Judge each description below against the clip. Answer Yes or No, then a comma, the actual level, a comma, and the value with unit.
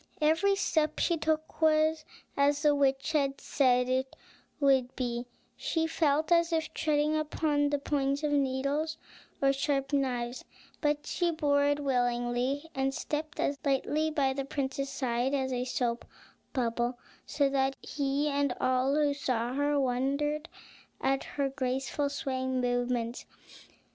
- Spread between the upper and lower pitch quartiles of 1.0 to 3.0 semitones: Yes, narrow, 2.4 semitones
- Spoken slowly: No, average, 145 wpm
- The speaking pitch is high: Yes, very high, 280 Hz